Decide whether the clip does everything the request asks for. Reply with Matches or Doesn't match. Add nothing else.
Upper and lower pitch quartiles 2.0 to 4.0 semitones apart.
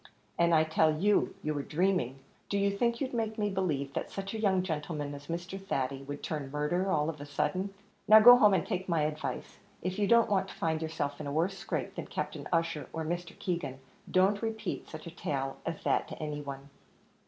Doesn't match